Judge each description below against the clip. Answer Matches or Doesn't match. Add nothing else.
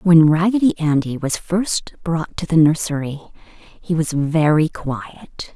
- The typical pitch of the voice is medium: Matches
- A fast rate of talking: Doesn't match